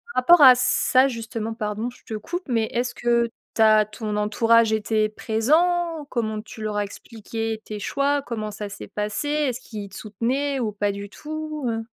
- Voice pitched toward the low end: No, high, 225 Hz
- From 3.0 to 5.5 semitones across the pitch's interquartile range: Yes, average, 3.5 semitones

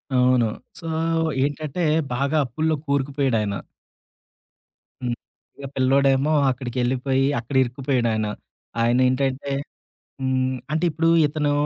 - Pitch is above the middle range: No, low, 130 Hz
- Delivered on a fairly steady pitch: Yes, narrow, 2.2 semitones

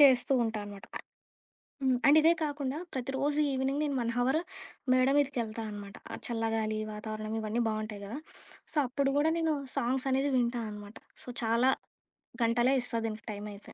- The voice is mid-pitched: No, high, 240 Hz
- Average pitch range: Yes, average, 3.9 semitones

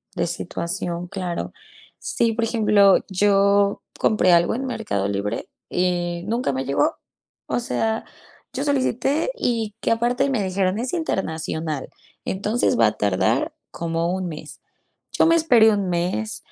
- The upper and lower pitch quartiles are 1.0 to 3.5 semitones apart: No, average, 5.2 semitones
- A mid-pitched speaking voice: No, high, 200 Hz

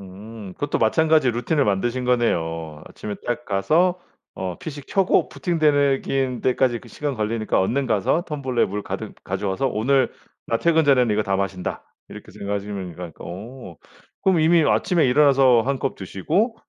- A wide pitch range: Yes, wide, 6.3 semitones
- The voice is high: No, low, 120 Hz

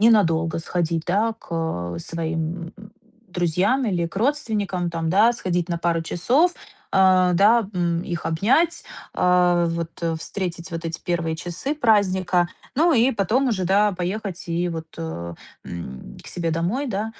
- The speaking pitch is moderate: Yes, medium, 180 Hz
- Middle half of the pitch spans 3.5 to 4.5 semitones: Yes, average, 4.0 semitones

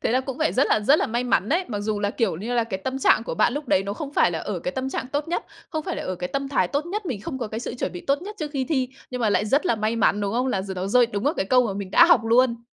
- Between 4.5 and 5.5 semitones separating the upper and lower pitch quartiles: Yes, average, 5.2 semitones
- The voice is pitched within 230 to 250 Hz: Yes, high, 245 Hz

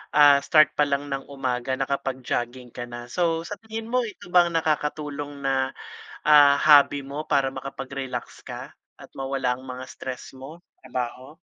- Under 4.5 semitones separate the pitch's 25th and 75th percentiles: Yes, narrow, 2.6 semitones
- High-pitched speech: No, medium, 140 Hz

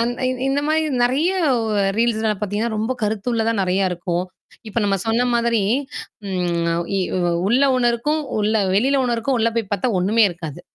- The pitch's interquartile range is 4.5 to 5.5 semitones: No, average, 3.7 semitones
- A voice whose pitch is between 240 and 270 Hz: No, high, 225 Hz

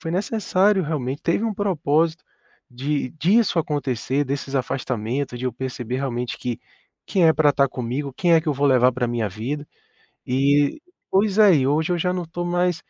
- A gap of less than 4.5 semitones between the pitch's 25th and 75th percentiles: No, average, 5.3 semitones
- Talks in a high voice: No, medium, 145 Hz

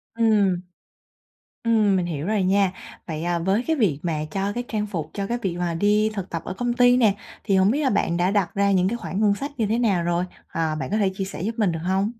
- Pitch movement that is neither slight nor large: Yes, average, 3.8 semitones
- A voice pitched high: Yes, high, 195 Hz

